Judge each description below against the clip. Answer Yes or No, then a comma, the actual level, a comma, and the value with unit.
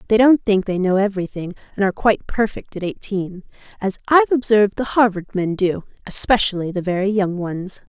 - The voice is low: No, high, 200 Hz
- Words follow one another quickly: No, average, 180 wpm